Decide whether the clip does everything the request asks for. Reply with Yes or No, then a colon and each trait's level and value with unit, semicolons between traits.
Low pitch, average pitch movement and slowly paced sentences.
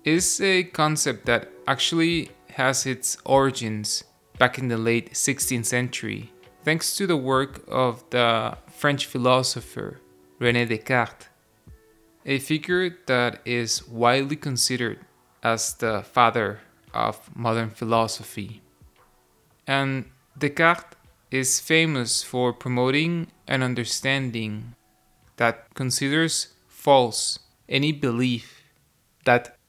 Yes: low, 125 Hz; average, 3.8 semitones; slow, 100 wpm